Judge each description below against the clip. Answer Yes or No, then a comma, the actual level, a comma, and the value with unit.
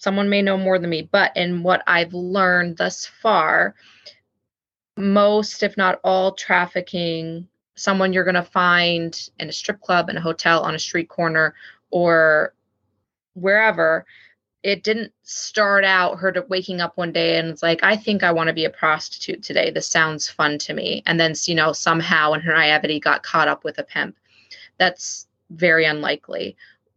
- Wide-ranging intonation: No, average, 2.7 semitones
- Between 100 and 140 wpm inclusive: No, average, 175 wpm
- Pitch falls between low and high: Yes, medium, 175 Hz